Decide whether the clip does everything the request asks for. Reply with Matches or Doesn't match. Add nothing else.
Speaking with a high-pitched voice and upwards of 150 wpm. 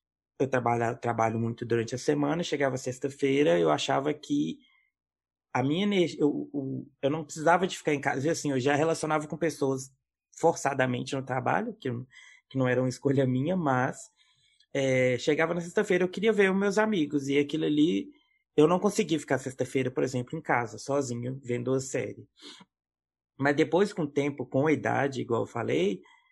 Doesn't match